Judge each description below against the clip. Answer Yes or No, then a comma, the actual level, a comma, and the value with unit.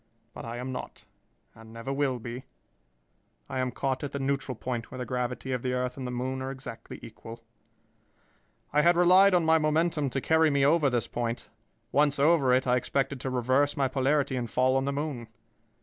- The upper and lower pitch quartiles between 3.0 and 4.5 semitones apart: No, narrow, 2.5 semitones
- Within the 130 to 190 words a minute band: No, average, 200 wpm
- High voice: No, low, 130 Hz